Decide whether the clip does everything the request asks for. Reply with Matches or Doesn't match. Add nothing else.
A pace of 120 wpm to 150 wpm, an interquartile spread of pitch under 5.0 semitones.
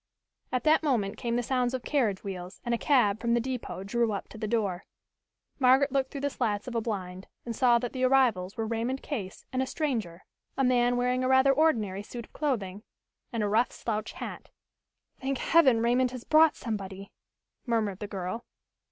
Doesn't match